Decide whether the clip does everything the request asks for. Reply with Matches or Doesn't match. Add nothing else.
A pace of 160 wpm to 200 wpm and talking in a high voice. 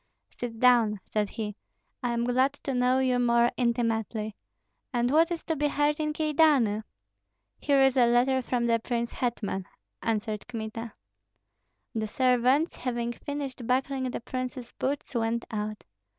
Doesn't match